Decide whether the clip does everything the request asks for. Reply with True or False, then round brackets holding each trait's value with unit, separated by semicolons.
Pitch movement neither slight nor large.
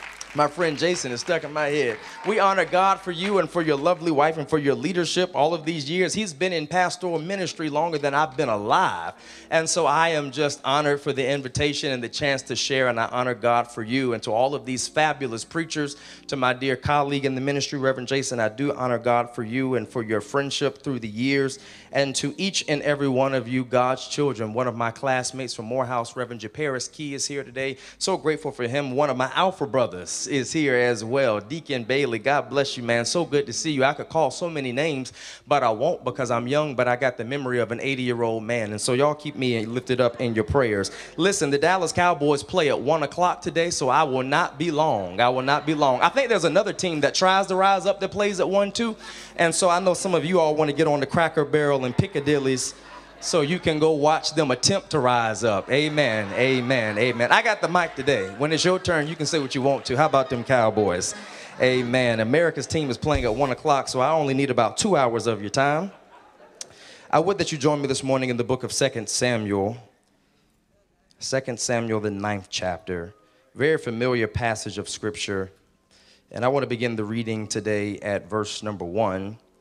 True (4.4 semitones)